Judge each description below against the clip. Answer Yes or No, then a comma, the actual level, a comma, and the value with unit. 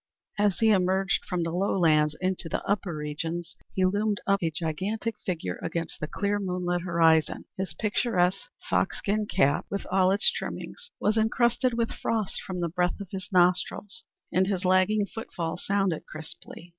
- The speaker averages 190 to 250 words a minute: No, average, 160 wpm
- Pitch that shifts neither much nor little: Yes, average, 3.1 semitones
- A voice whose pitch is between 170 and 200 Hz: Yes, medium, 185 Hz